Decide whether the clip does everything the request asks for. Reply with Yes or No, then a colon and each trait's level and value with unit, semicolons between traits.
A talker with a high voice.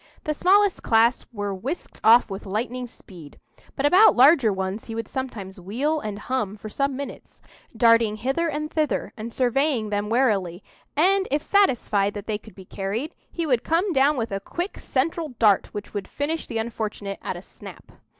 Yes: high, 235 Hz